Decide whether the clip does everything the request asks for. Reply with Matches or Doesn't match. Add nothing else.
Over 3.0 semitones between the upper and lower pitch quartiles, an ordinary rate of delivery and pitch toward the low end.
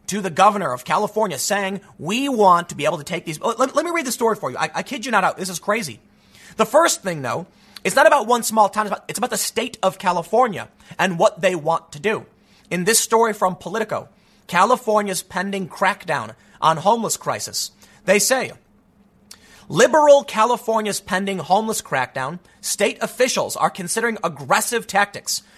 Doesn't match